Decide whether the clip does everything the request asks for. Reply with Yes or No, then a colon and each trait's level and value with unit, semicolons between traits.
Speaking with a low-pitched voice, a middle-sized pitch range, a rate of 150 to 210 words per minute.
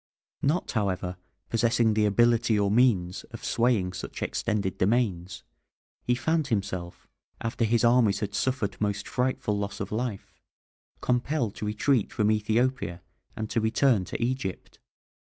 No: low, 110 Hz; average, 3.5 semitones; slow, 135 wpm